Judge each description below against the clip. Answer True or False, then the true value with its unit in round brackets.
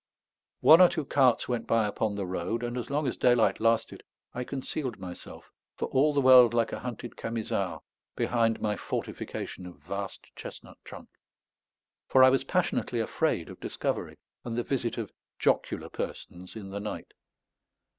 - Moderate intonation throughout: True (3.8 semitones)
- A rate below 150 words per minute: False (165 wpm)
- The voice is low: True (115 Hz)